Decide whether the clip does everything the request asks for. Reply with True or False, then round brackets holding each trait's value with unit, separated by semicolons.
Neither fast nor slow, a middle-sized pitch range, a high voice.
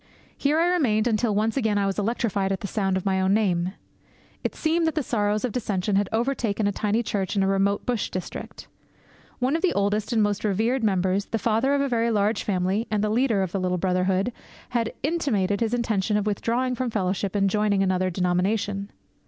False (210 wpm; 3.2 semitones; 210 Hz)